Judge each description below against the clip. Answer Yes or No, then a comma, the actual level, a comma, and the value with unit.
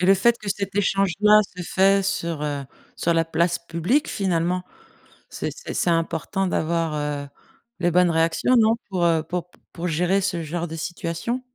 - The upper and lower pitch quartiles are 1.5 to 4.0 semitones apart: Yes, average, 2.9 semitones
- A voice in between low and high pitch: Yes, medium, 175 Hz